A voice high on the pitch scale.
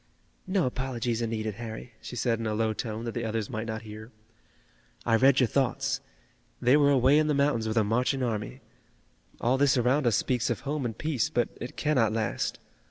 No: low, 120 Hz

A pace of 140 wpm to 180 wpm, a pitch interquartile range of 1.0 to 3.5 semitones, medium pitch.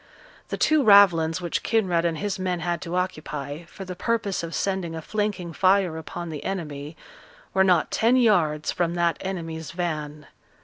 Yes: average, 170 wpm; average, 3.1 semitones; medium, 175 Hz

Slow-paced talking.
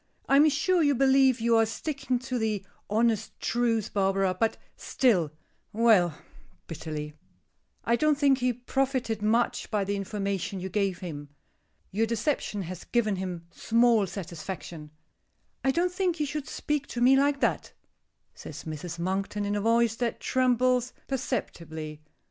No: average, 150 wpm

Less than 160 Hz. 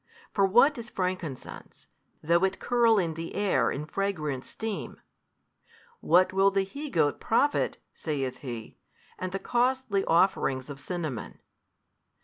No: medium, 185 Hz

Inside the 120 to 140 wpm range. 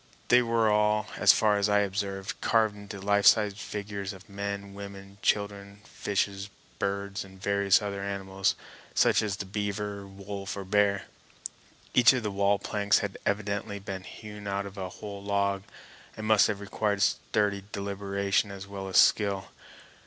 No: average, 165 wpm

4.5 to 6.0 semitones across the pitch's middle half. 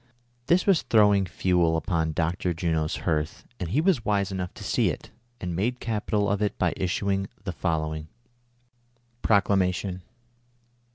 No: average, 3.7 semitones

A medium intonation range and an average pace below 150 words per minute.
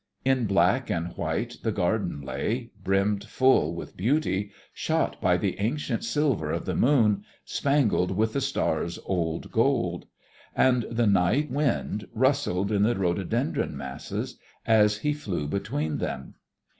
No: wide, 6.3 semitones; average, 140 wpm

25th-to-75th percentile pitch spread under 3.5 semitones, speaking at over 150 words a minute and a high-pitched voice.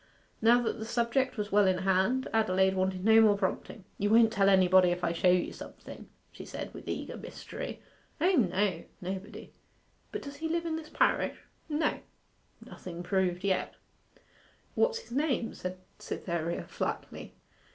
No: average, 4.7 semitones; average, 160 wpm; high, 200 Hz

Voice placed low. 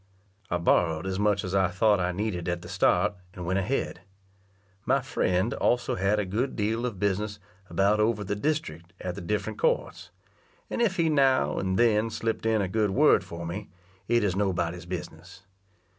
Yes: low, 100 Hz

